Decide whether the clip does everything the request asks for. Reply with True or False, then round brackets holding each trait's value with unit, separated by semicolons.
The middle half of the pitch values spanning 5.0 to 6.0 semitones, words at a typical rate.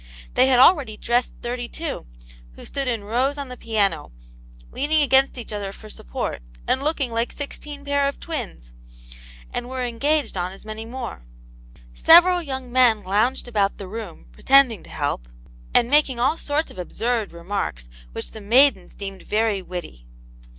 True (5.4 semitones; 165 wpm)